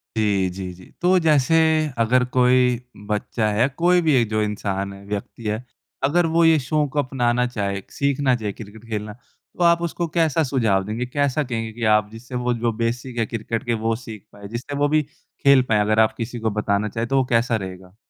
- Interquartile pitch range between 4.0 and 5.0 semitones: Yes, average, 4.3 semitones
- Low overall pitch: Yes, low, 120 Hz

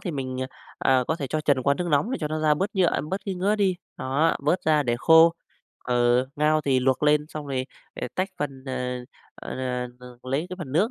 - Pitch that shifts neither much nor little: Yes, average, 4.3 semitones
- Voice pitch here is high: No, medium, 150 Hz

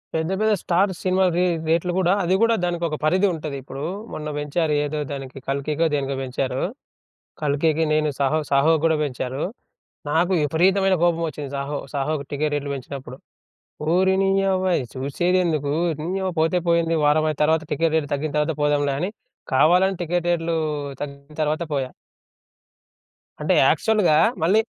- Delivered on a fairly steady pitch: No, average, 3.5 semitones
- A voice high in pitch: No, medium, 155 Hz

